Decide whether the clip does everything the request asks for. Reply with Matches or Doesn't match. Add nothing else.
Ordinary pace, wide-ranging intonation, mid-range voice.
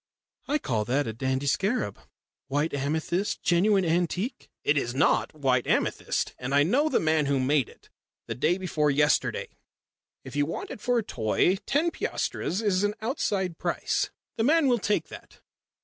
Matches